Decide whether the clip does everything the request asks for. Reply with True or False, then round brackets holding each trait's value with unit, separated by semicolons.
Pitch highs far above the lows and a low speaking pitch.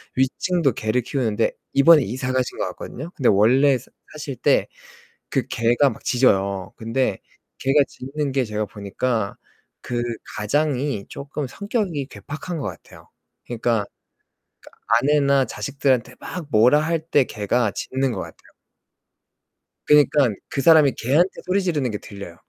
False (4.4 semitones; 130 Hz)